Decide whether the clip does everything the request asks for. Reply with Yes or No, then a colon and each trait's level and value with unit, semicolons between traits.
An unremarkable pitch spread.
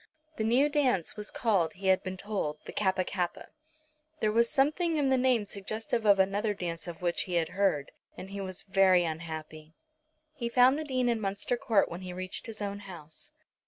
Yes: average, 4.5 semitones